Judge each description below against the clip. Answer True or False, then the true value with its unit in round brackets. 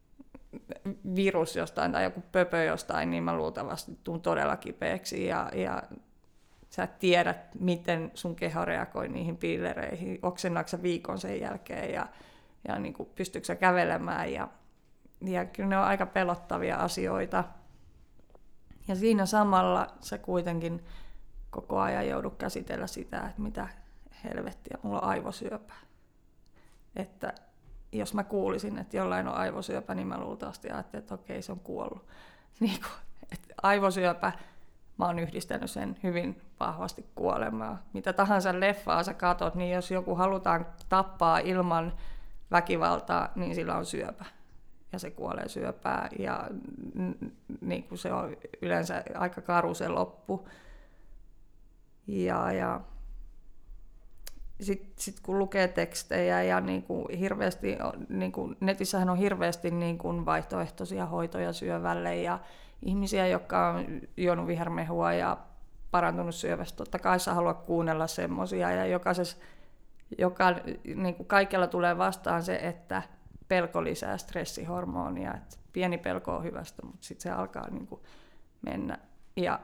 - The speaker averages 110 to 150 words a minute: True (125 wpm)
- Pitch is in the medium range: True (175 Hz)